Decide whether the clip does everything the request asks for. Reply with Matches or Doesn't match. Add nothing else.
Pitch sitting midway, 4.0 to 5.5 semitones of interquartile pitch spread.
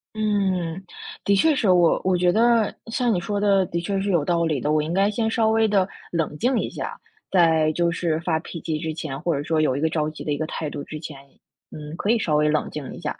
Matches